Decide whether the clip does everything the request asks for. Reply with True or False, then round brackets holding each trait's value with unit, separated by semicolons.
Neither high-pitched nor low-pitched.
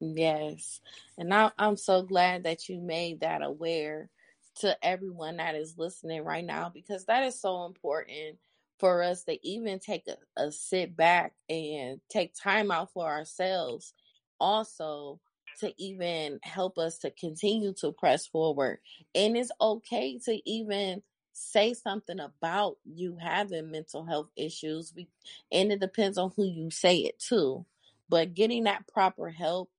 True (180 Hz)